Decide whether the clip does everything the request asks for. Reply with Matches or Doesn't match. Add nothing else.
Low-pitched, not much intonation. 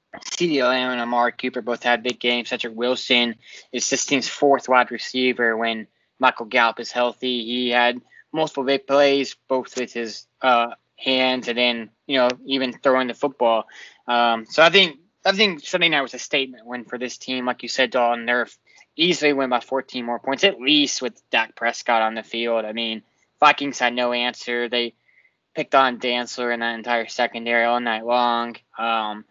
Matches